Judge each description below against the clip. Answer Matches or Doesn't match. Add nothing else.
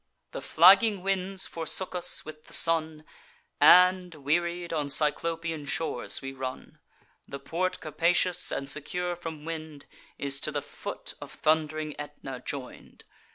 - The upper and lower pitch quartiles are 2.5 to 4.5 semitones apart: Matches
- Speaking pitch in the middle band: Matches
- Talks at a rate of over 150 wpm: Doesn't match